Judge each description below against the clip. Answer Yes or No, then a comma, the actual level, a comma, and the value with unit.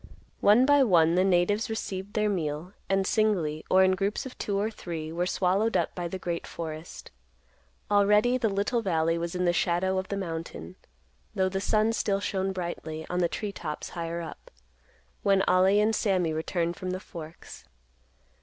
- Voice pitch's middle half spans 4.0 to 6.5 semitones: No, average, 3.2 semitones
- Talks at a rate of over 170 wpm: Yes, average, 180 wpm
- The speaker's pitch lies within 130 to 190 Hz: Yes, medium, 185 Hz